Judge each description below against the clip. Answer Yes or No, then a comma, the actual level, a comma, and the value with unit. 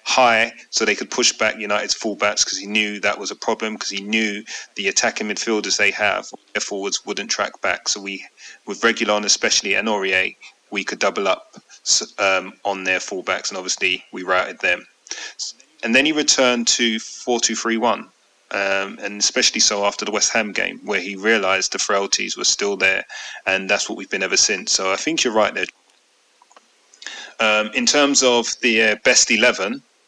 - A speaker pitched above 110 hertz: No, low, 105 Hz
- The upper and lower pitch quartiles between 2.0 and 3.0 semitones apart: Yes, narrow, 2.5 semitones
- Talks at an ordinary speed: Yes, average, 185 wpm